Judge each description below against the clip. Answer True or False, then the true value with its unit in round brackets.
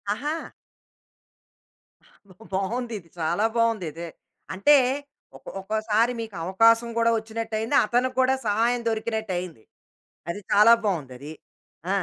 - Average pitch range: True (3.6 semitones)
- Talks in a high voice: True (220 Hz)